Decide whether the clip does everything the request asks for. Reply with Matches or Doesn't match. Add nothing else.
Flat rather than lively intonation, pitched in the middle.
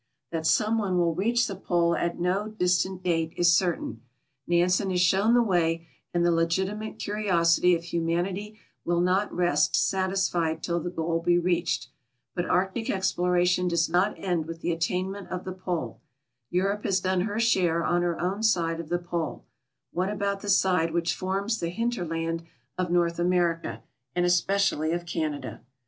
Matches